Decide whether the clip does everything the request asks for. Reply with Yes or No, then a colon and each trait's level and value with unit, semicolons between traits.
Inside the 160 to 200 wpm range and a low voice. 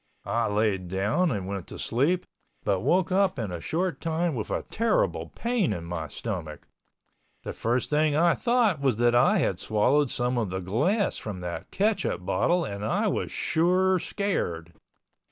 Yes: average, 170 wpm; low, 125 Hz